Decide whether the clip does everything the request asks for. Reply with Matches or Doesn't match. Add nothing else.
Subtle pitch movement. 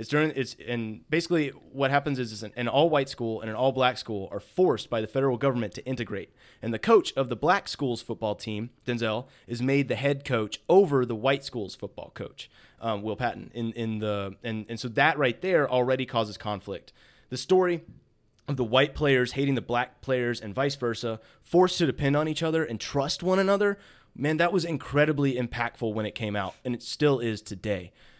Doesn't match